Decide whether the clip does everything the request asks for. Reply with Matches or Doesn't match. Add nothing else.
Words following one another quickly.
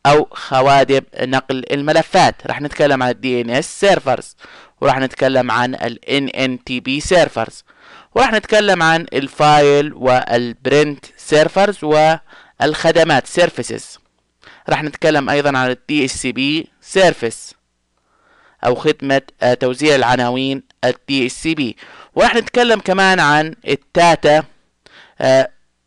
Doesn't match